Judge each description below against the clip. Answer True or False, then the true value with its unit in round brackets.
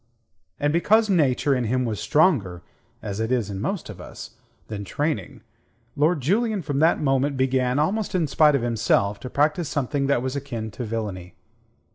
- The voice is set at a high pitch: False (135 Hz)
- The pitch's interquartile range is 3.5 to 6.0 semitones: True (5.4 semitones)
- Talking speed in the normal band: True (175 wpm)